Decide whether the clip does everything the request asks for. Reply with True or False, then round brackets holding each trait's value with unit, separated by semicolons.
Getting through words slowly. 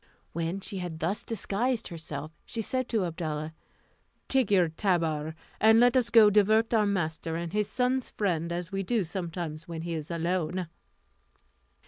False (165 wpm)